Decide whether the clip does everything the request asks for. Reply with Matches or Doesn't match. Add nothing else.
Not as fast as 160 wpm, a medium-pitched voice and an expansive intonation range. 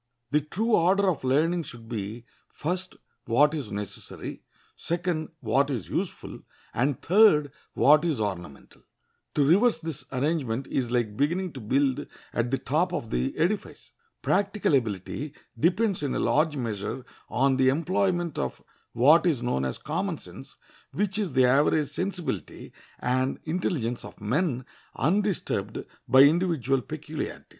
Matches